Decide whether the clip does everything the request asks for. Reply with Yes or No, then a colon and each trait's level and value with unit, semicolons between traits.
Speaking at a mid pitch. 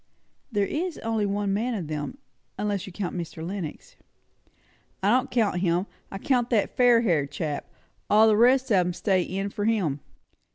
No: high, 205 Hz